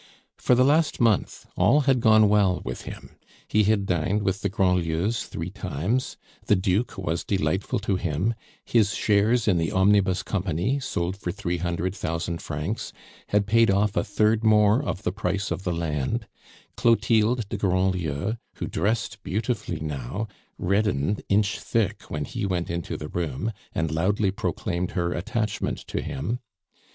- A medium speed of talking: Yes, average, 160 wpm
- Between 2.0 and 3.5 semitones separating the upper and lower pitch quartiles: No, average, 3.9 semitones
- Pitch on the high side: No, low, 100 Hz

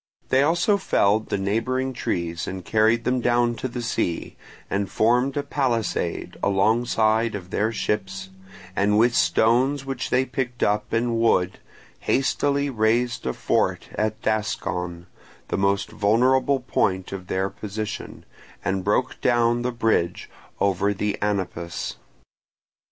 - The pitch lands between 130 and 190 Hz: No, low, 110 Hz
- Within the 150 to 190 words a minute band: No, slow, 135 wpm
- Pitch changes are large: No, average, 3.8 semitones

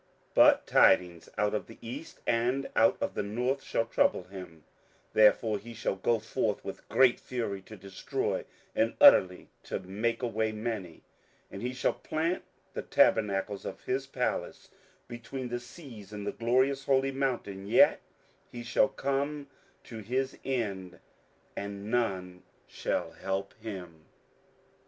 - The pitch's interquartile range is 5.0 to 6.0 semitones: No, average, 4.5 semitones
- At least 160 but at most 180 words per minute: No, average, 145 wpm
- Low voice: Yes, low, 115 Hz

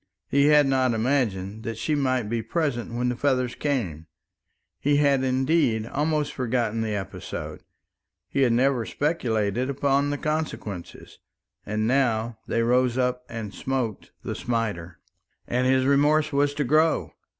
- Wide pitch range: No, average, 3.8 semitones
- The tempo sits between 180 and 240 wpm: No, average, 145 wpm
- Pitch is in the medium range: No, low, 125 Hz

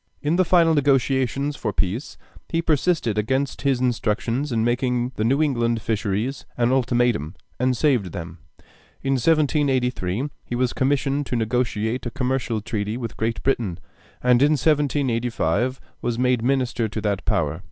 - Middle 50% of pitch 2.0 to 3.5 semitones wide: Yes, average, 3.2 semitones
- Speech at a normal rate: Yes, average, 150 wpm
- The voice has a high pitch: No, low, 125 Hz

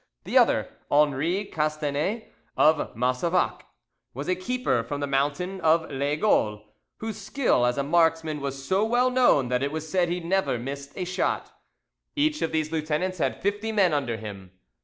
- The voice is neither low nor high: Yes, medium, 155 Hz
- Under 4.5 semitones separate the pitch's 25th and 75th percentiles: No, average, 5.2 semitones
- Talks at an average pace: Yes, average, 165 wpm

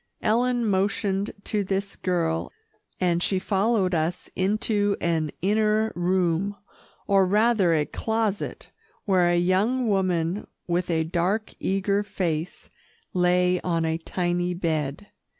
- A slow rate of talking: Yes, slow, 120 wpm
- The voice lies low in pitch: No, medium, 185 Hz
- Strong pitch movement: No, average, 2.9 semitones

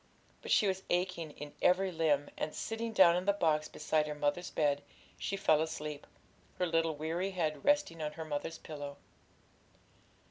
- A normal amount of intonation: Yes, average, 3.2 semitones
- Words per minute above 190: No, average, 170 wpm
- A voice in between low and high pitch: Yes, medium, 160 Hz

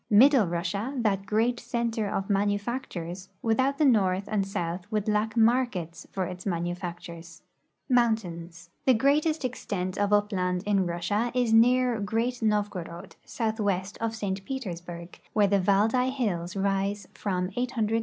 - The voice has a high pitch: Yes, high, 205 Hz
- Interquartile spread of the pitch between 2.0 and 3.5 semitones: No, average, 4.1 semitones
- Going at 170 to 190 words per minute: No, average, 150 wpm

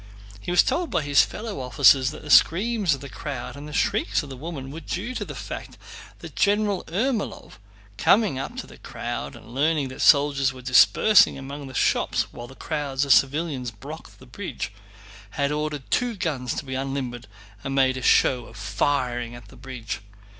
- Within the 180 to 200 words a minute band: Yes, average, 190 wpm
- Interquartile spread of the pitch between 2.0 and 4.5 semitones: Yes, average, 4.0 semitones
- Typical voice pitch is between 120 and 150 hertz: Yes, medium, 140 Hz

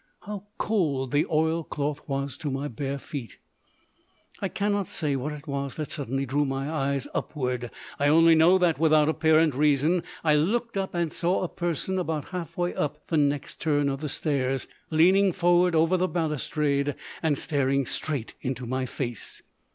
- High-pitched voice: No, medium, 150 Hz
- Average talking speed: Yes, average, 170 wpm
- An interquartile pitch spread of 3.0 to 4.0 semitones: Yes, average, 3.4 semitones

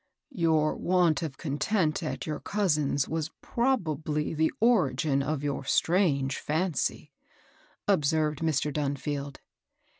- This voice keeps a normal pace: No, slow, 115 wpm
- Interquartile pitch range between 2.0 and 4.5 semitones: Yes, average, 2.8 semitones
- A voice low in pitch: No, medium, 155 Hz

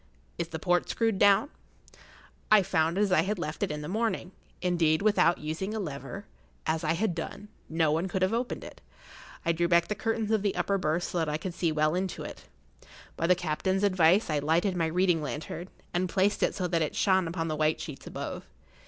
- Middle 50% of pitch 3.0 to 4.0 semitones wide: Yes, average, 3.4 semitones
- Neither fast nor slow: No, fast, 220 wpm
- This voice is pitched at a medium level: Yes, medium, 175 Hz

